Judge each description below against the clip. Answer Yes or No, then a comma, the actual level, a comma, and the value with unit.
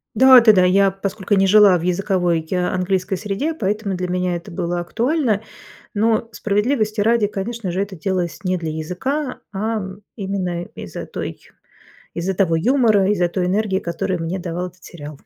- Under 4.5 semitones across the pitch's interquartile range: Yes, average, 3.1 semitones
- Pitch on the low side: No, high, 190 Hz